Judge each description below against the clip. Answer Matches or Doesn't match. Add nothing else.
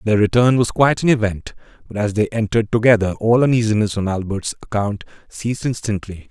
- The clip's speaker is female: Doesn't match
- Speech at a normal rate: Matches